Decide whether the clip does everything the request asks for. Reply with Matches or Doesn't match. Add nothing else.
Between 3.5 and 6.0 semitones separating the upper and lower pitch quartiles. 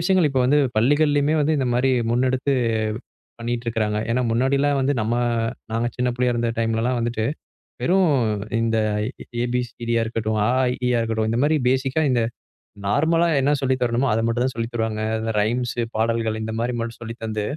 Doesn't match